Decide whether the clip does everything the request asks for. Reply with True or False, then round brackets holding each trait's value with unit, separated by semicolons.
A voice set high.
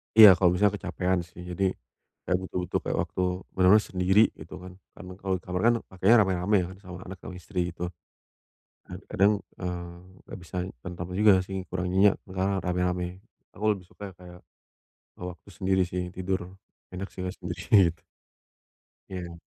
False (90 Hz)